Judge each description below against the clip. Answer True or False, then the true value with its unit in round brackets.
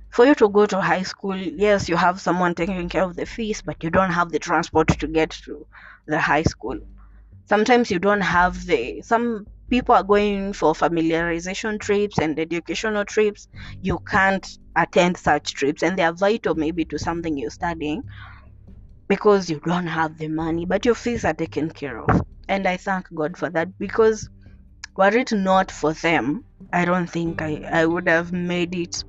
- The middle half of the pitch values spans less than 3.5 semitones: False (4.1 semitones)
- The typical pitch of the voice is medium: True (175 Hz)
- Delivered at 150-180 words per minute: False (190 wpm)